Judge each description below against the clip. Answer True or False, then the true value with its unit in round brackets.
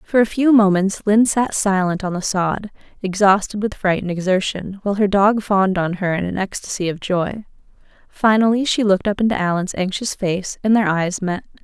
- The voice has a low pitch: False (195 Hz)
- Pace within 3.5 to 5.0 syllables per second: False (5.3 syllables/s)